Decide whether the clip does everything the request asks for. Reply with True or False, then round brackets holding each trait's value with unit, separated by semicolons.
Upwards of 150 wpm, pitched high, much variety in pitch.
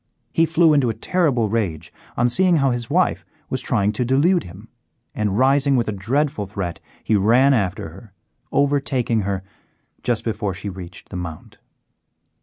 False (165 wpm; 115 Hz; 5.8 semitones)